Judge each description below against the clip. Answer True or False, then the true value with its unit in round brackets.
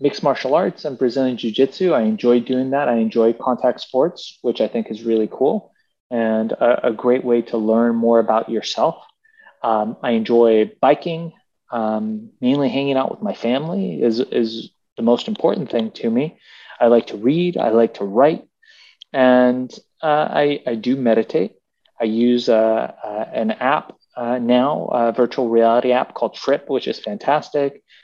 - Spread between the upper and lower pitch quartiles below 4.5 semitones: True (3.1 semitones)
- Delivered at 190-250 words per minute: False (175 wpm)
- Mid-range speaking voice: False (120 Hz)